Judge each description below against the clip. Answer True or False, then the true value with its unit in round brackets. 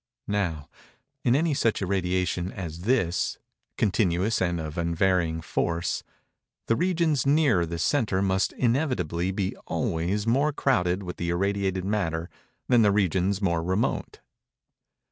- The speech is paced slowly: True (120 wpm)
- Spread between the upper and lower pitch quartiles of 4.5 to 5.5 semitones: True (4.8 semitones)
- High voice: False (95 Hz)